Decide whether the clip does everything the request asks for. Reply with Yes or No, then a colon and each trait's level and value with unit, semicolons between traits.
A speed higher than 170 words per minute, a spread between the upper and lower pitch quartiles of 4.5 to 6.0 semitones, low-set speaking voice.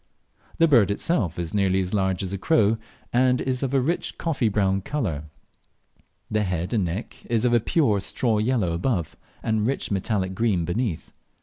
Yes: average, 180 wpm; average, 4.8 semitones; low, 105 Hz